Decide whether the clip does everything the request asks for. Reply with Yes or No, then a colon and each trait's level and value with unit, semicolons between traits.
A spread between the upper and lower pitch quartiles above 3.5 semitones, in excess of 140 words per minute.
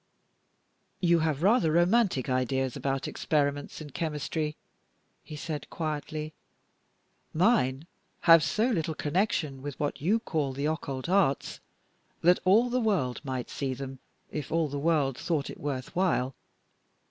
No: average, 4.0 semitones; slow, 135 wpm